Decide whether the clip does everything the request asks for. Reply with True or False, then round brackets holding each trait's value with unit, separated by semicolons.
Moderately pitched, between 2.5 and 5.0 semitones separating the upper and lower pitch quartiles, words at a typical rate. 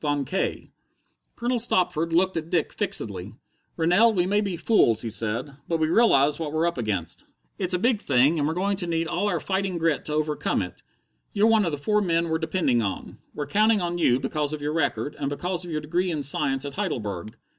False (160 Hz; 4.6 semitones; 220 wpm)